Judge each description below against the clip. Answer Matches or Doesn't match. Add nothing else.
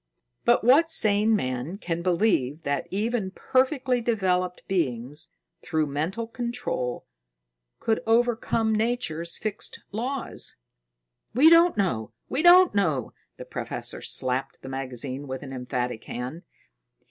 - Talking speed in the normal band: Doesn't match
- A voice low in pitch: Doesn't match